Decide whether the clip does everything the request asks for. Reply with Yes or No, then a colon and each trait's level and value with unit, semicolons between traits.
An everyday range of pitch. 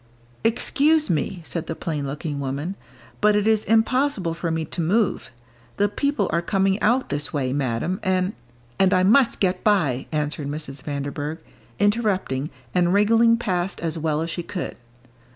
No: wide, 5.8 semitones